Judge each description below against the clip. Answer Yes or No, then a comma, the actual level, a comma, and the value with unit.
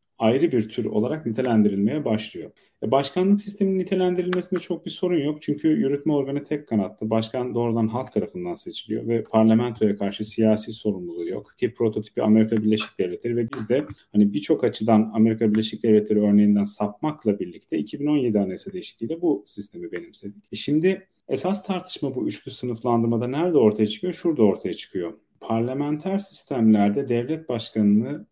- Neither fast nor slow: No, fast, 150 wpm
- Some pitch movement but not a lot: No, wide, 6.0 semitones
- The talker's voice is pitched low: Yes, low, 115 Hz